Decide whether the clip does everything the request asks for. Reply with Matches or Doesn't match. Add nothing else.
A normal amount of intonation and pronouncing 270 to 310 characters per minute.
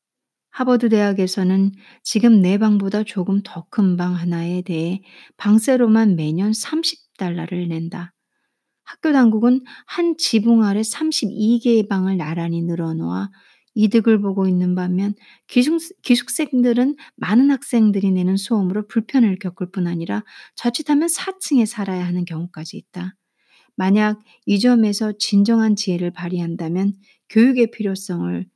Matches